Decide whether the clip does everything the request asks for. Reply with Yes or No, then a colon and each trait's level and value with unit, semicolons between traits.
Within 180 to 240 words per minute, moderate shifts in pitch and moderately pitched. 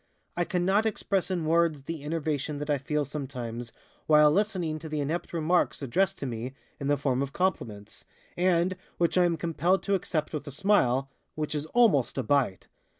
Yes: average, 185 wpm; average, 4.1 semitones; medium, 155 Hz